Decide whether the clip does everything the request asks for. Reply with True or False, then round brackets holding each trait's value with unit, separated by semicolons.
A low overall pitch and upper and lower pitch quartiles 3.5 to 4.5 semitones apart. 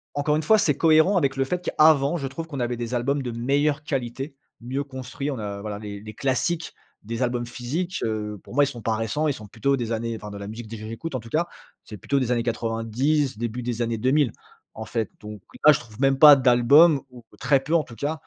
True (125 Hz; 4.2 semitones)